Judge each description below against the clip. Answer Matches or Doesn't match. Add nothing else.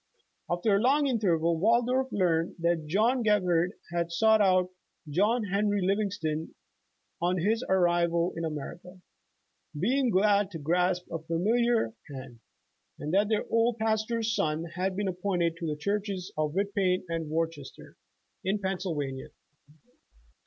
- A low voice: Doesn't match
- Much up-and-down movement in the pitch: Doesn't match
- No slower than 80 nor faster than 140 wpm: Matches